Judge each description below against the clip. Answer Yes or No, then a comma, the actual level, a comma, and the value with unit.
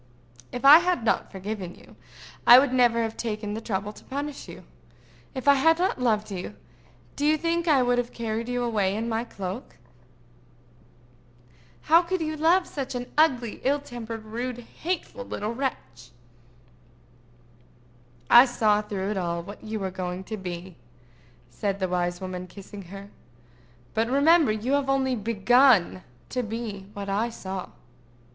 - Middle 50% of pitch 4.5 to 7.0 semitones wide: Yes, average, 5.1 semitones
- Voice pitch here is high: Yes, high, 230 Hz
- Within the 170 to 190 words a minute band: No, average, 160 wpm